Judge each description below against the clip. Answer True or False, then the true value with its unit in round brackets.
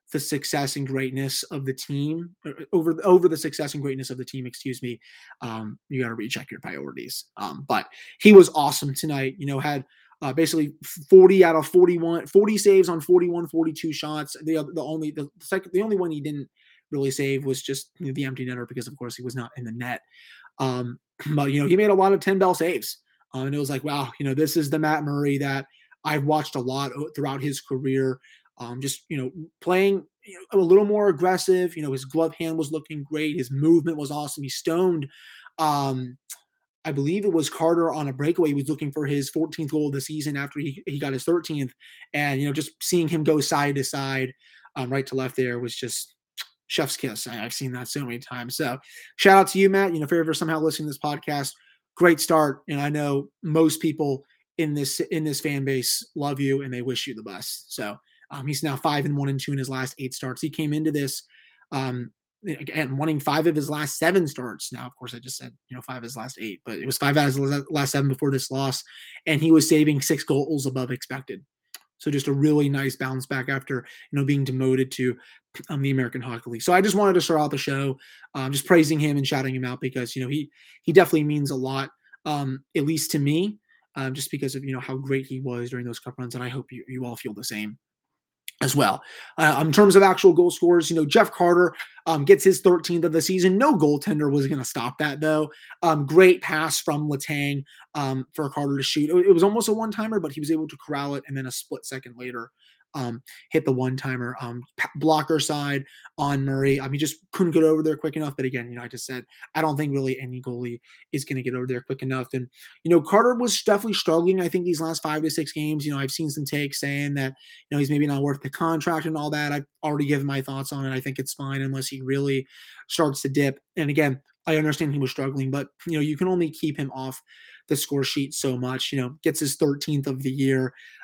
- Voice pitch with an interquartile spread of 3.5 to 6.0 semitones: False (3.1 semitones)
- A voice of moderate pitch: True (145 Hz)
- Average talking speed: False (240 wpm)